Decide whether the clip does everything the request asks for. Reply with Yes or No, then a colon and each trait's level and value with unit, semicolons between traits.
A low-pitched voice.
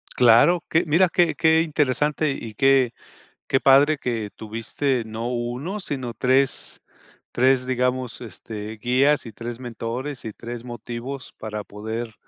Yes: low, 125 Hz